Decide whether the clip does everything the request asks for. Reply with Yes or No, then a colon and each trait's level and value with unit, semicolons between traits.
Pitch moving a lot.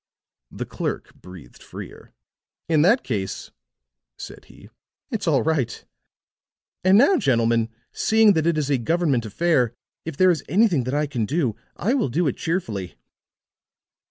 Yes: wide, 7.0 semitones